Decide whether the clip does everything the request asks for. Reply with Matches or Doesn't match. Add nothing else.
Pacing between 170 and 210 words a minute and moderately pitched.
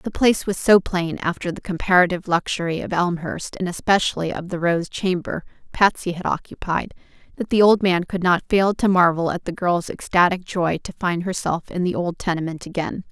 Matches